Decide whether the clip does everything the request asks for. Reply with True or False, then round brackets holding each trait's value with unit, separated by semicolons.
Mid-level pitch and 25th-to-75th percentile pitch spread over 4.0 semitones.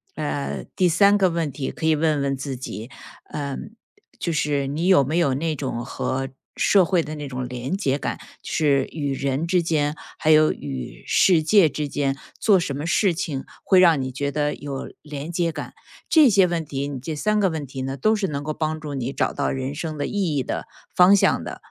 False (150 Hz; 3.7 semitones)